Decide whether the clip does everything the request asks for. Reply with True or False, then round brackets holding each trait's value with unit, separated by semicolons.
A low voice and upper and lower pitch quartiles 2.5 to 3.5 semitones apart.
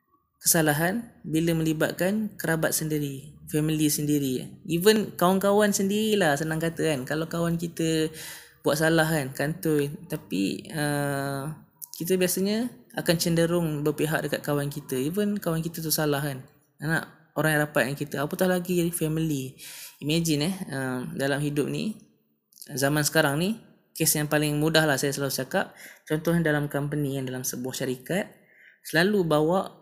False (155 Hz; 2.8 semitones)